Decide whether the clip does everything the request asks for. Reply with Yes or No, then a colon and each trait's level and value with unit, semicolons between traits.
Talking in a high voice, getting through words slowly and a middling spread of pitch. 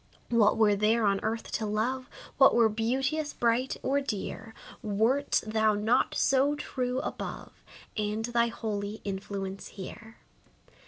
Yes: high, 225 Hz; slow, 130 wpm; average, 3.1 semitones